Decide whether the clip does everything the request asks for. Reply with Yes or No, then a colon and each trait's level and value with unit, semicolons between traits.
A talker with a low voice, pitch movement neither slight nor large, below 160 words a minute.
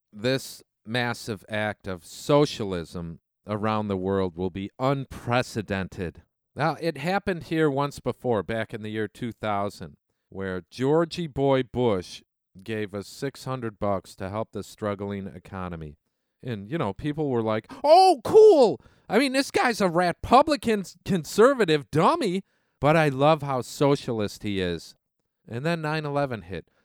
No: low, 120 Hz; wide, 7.6 semitones; average, 145 wpm